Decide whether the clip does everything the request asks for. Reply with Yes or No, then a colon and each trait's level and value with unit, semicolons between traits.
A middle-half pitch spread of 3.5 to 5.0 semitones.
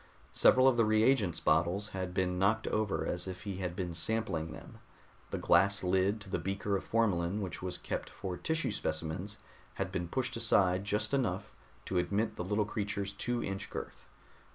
No: average, 3.1 semitones